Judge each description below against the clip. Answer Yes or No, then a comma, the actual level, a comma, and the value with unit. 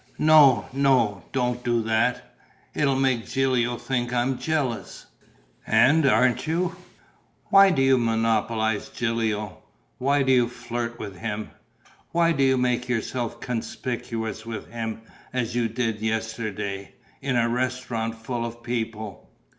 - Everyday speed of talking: No, slow, 130 wpm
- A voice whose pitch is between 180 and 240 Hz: No, low, 120 Hz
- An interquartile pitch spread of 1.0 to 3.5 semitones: Yes, narrow, 2.6 semitones